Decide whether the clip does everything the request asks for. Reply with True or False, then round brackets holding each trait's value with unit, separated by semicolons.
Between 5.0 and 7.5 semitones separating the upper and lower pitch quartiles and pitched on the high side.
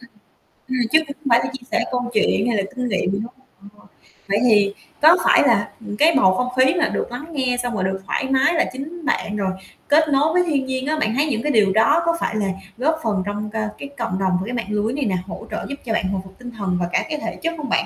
True (5.4 semitones; 240 Hz)